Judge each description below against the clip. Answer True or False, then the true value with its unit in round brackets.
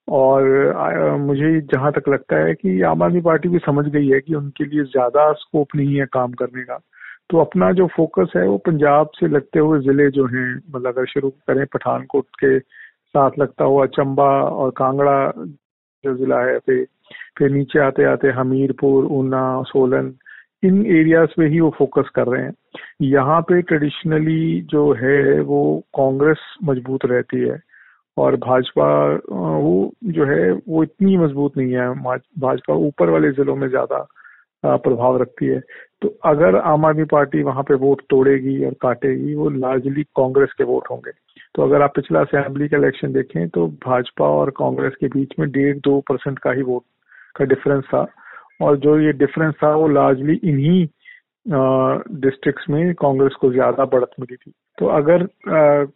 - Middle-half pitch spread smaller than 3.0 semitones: True (2.6 semitones)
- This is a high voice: False (140 Hz)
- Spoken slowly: False (170 wpm)